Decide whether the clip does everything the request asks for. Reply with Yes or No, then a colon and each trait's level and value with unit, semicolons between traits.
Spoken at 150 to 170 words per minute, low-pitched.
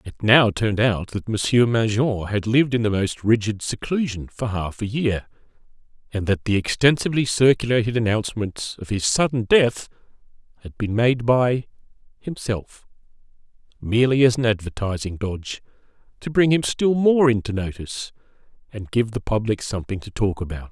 Yes: average, 155 wpm; low, 115 Hz